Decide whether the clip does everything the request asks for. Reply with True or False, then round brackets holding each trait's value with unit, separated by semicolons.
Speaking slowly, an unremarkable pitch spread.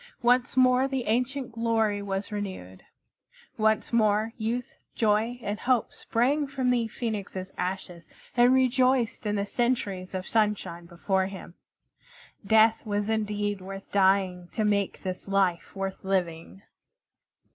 True (130 wpm; 3.7 semitones)